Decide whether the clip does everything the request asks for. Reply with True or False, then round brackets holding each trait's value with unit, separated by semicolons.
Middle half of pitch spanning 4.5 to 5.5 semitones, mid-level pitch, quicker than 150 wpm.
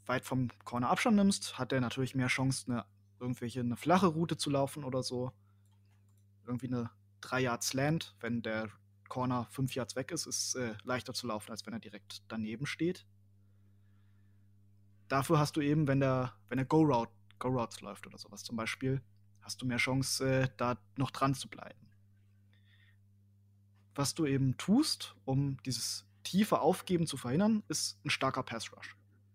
False (4.9 semitones; 120 Hz; 165 wpm)